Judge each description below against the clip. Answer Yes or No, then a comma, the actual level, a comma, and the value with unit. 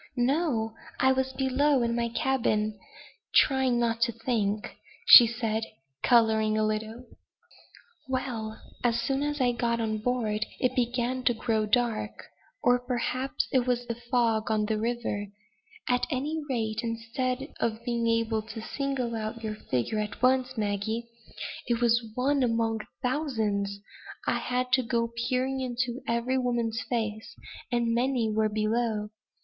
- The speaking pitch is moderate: No, high, 235 Hz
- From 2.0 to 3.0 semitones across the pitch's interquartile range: Yes, narrow, 2.4 semitones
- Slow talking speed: No, average, 145 wpm